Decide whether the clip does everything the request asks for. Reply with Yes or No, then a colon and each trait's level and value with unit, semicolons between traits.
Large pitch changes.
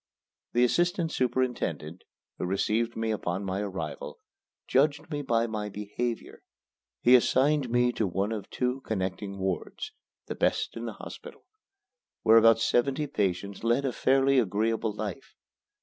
No: average, 4.1 semitones